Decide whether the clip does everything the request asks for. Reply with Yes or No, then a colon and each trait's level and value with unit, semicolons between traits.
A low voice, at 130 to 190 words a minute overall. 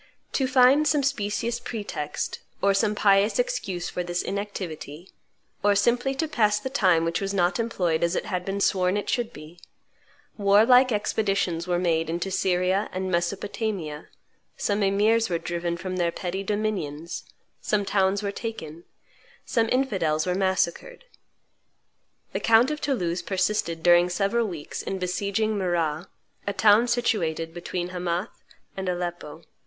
No: high, 195 Hz; average, 150 wpm